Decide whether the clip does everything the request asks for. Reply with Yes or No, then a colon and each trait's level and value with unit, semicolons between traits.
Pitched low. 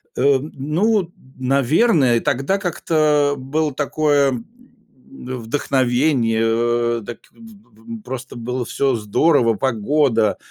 Yes: low, 130 Hz